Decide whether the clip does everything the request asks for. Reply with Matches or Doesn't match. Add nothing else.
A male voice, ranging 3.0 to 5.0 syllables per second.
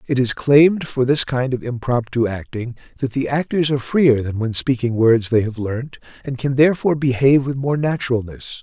Doesn't match